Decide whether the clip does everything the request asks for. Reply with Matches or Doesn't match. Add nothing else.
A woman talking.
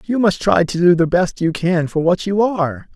Doesn't match